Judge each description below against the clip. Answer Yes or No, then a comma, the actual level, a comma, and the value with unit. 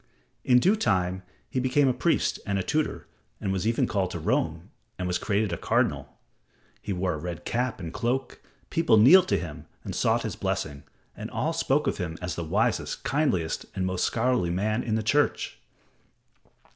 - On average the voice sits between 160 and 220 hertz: No, low, 105 Hz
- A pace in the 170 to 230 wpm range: Yes, average, 185 wpm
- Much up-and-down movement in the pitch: Yes, wide, 6.0 semitones